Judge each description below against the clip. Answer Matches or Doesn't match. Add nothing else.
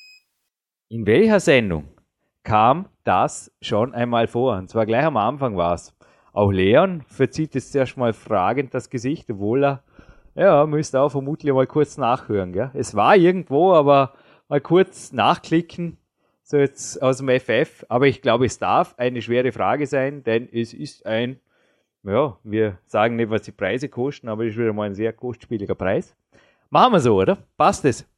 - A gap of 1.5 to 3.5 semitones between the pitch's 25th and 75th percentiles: Doesn't match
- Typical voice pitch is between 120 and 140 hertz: Matches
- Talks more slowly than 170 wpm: Doesn't match